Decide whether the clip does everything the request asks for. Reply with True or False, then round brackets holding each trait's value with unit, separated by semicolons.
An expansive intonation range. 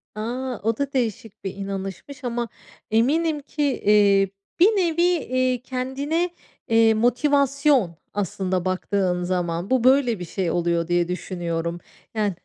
True (6.3 semitones)